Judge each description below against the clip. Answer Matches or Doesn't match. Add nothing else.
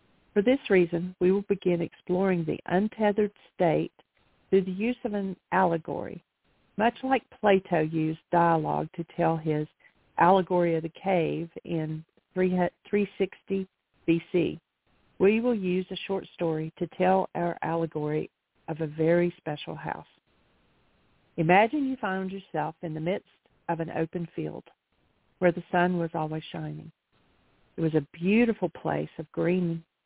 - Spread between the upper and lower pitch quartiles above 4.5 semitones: Doesn't match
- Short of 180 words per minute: Matches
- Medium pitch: Matches